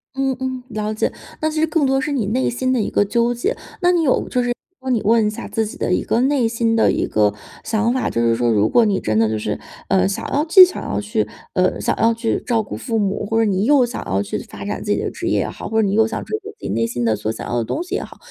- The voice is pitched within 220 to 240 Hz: Yes, high, 225 Hz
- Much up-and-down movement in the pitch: Yes, wide, 5.9 semitones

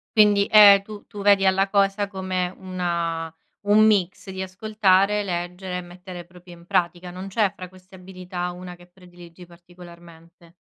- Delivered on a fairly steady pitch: Yes, narrow, 1.9 semitones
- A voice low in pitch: No, medium, 185 Hz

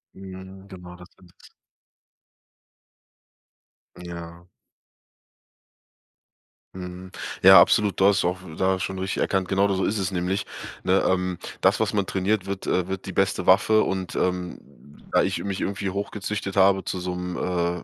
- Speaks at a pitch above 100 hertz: No, very low, 95 Hz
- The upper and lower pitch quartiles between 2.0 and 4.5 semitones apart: No, narrow, 1.4 semitones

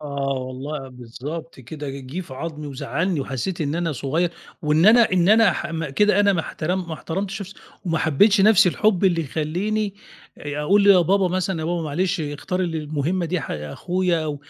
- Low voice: No, medium, 165 Hz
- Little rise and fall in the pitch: No, average, 4.4 semitones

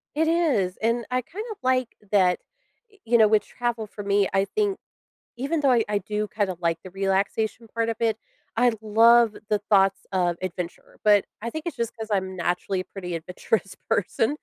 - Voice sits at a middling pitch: No, high, 215 Hz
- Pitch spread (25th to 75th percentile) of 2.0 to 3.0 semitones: No, average, 3.7 semitones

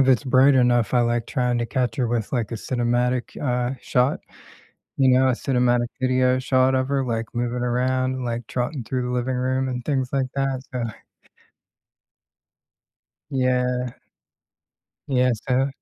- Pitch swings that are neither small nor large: No, narrow, 1.1 semitones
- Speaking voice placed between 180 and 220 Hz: No, low, 125 Hz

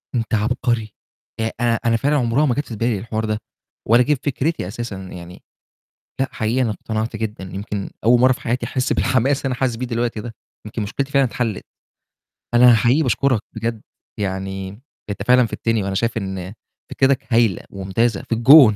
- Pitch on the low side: Yes, low, 115 Hz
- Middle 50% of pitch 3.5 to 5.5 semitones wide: No, average, 3.0 semitones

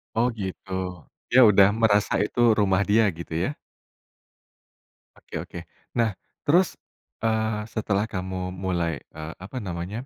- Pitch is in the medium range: No, low, 100 Hz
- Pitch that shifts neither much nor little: Yes, average, 3.2 semitones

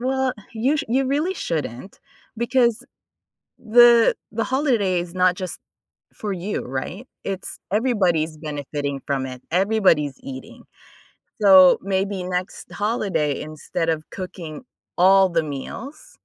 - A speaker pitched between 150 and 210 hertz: Yes, high, 190 Hz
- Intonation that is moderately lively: No, wide, 6.7 semitones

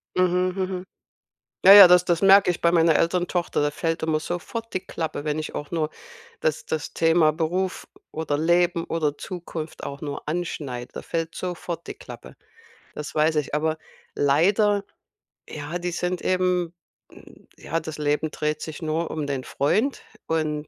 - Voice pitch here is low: No, medium, 165 Hz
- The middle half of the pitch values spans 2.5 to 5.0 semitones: Yes, average, 2.8 semitones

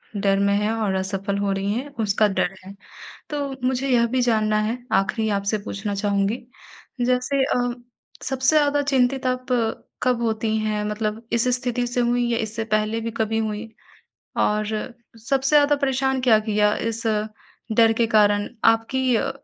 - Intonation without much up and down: No, average, 3.2 semitones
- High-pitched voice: Yes, high, 225 Hz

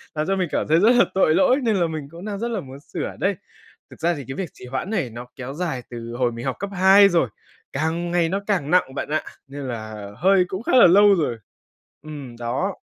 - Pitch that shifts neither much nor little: No, wide, 6.4 semitones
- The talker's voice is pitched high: No, medium, 160 Hz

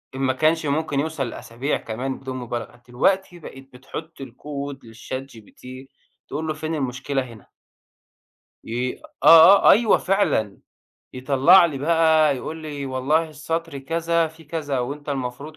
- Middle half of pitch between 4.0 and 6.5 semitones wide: No, average, 3.5 semitones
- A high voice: No, medium, 140 Hz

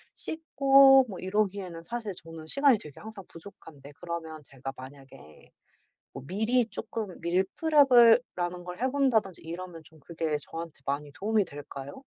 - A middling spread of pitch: No, wide, 6.2 semitones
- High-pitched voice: No, medium, 180 Hz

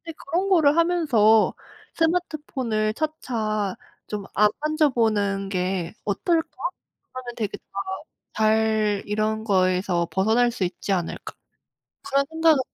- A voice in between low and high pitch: No, high, 220 Hz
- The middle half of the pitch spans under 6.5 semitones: No, wide, 6.9 semitones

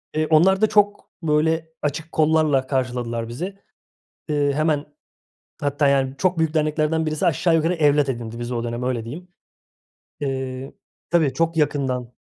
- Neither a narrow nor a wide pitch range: Yes, average, 3.5 semitones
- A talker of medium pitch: Yes, medium, 150 Hz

